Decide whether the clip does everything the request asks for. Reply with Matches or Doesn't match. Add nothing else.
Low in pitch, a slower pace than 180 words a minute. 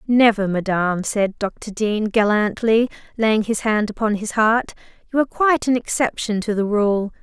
Doesn't match